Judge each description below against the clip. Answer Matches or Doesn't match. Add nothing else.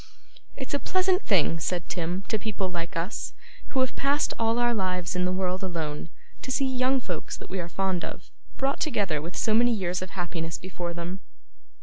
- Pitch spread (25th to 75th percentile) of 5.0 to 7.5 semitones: Matches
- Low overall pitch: Doesn't match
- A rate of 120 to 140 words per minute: Doesn't match